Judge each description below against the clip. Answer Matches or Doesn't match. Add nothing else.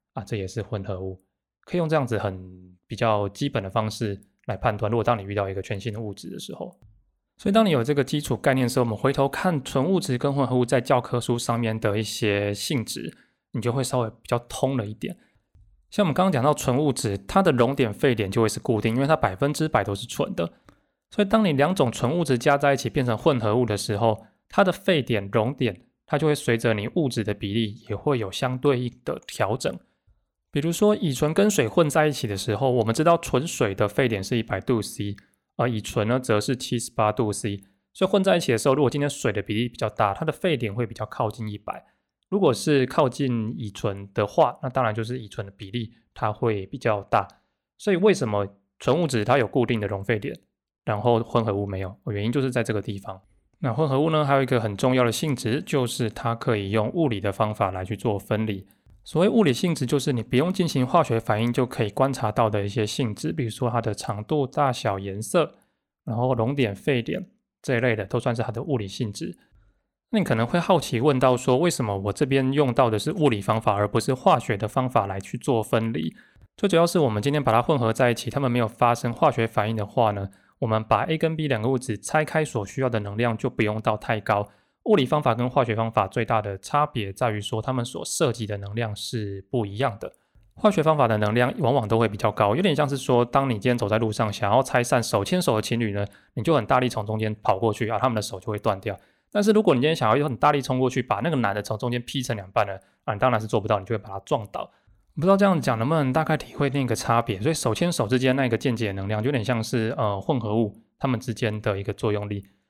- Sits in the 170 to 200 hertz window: Doesn't match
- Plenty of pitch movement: Doesn't match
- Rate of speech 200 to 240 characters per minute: Doesn't match